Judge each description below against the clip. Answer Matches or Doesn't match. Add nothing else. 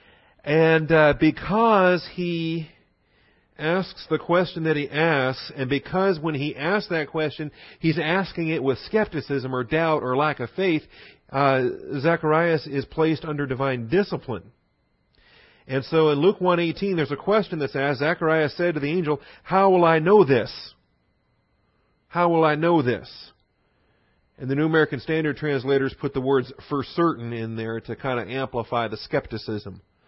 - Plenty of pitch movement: Doesn't match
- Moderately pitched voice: Matches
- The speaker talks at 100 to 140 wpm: Doesn't match